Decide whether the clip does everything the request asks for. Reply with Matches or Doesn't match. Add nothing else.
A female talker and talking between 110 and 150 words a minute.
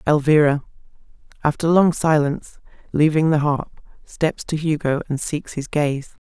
Matches